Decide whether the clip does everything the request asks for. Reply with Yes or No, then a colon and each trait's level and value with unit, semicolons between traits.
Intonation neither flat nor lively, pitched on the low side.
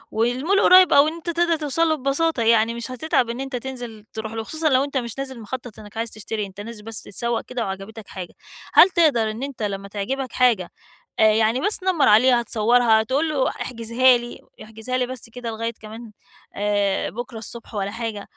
No: average, 3.3 semitones; high, 235 Hz